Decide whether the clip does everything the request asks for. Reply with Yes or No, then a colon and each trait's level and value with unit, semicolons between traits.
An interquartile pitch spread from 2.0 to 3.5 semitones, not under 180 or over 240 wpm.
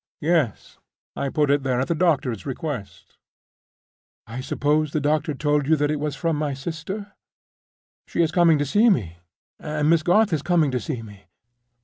No: average, 3.2 semitones; average, 170 wpm